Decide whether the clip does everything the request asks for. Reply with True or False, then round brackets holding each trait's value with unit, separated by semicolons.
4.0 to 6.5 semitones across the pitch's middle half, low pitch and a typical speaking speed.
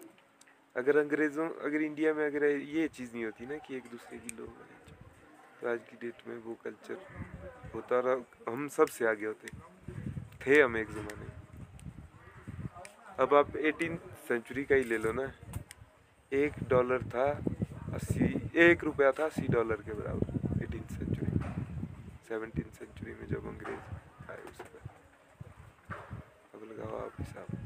True (4.8 semitones; 125 Hz; 150 wpm)